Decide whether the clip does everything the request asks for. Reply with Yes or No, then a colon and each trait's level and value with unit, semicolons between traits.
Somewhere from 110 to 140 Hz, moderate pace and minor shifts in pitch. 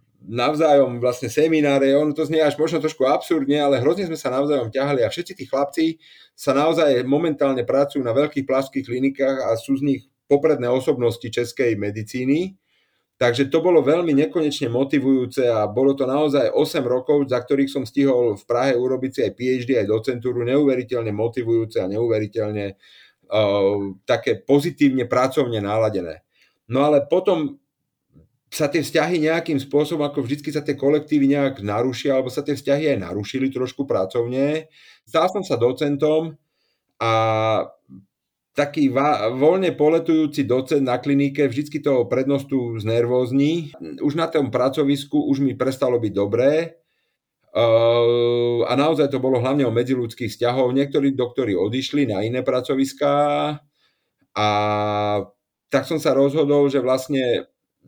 No: low, 135 Hz; average, 140 wpm; average, 3.2 semitones